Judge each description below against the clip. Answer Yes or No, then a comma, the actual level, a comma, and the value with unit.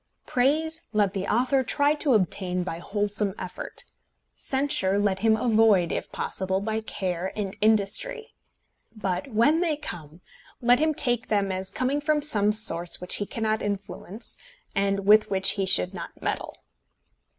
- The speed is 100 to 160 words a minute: Yes, average, 150 wpm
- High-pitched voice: Yes, high, 210 Hz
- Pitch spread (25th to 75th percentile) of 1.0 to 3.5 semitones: No, average, 4.8 semitones